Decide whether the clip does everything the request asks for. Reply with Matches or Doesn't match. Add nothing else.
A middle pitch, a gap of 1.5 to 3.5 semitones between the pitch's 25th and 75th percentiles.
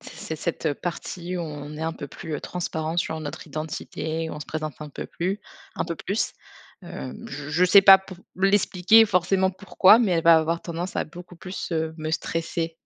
Matches